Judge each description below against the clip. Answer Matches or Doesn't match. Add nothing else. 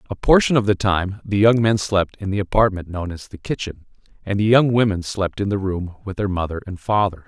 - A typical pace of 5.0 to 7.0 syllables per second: Matches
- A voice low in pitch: Matches